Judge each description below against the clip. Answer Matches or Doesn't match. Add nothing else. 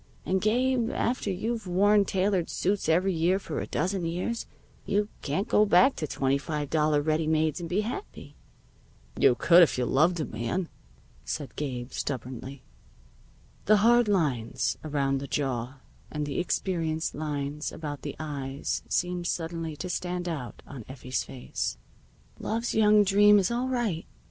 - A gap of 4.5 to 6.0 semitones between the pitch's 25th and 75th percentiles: Matches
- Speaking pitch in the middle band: Matches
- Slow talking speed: Doesn't match